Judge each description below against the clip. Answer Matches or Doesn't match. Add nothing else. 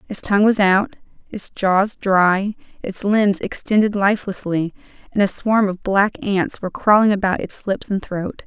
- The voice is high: Matches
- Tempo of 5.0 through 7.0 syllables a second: Doesn't match